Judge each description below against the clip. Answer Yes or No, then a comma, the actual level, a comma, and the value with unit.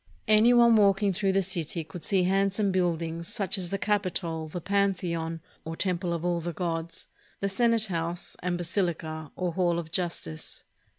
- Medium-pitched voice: Yes, medium, 180 Hz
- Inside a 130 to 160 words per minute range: No, average, 175 wpm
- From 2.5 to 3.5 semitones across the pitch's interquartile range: Yes, average, 2.9 semitones